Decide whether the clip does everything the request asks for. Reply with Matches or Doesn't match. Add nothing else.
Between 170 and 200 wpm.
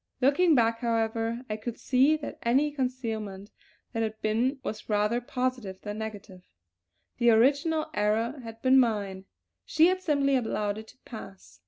Doesn't match